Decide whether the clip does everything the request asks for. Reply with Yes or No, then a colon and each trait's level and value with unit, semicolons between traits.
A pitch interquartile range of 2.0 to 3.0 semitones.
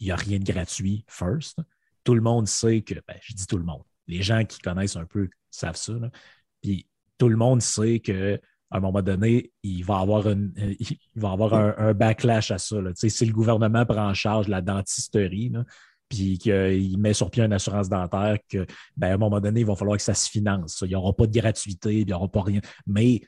Yes: narrow, 2.5 semitones